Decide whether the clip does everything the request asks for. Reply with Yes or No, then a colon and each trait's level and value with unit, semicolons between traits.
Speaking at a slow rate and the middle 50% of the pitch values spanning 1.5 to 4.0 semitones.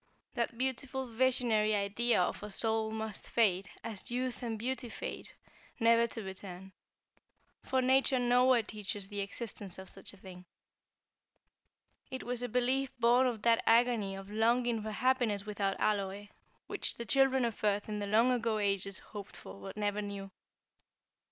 No: average, 160 wpm; average, 3.3 semitones